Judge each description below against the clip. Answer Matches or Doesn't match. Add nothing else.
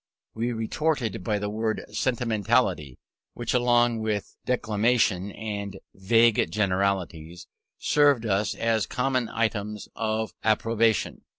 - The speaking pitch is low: Matches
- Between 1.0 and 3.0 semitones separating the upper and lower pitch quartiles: Matches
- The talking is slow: Matches